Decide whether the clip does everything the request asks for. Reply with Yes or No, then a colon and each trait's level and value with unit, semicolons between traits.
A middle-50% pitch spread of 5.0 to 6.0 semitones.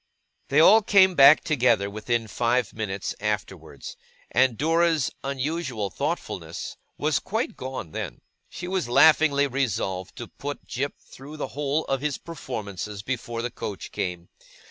Yes: average, 5.3 semitones